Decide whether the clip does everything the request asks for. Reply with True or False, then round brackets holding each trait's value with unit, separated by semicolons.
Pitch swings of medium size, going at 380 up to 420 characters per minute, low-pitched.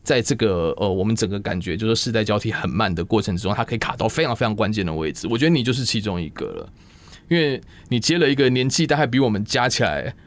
True (4.1 semitones; 385 characters per minute; 110 Hz)